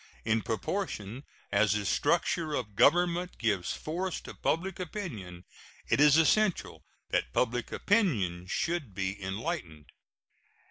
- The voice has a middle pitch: No, low, 125 Hz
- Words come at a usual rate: No, slow, 125 wpm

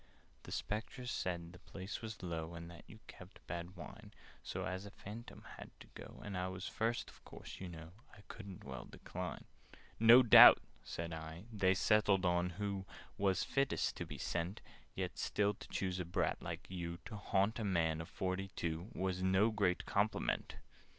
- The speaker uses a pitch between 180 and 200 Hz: No, very low, 95 Hz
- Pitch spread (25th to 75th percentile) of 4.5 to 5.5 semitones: No, average, 3.1 semitones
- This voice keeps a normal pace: Yes, average, 180 wpm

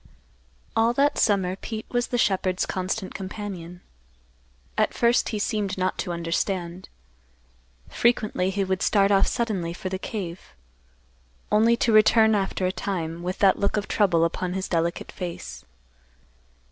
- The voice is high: Yes, high, 195 Hz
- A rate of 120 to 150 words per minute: Yes, average, 145 wpm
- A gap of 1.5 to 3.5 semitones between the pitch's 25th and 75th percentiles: Yes, average, 3.0 semitones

